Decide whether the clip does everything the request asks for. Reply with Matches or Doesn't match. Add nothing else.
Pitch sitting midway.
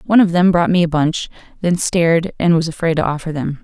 Matches